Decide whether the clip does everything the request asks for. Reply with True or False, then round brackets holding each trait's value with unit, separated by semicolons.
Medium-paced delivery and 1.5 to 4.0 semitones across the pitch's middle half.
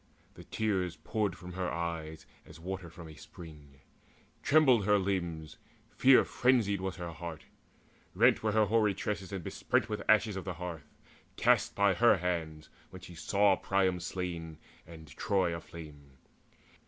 True (155 wpm; 3.6 semitones)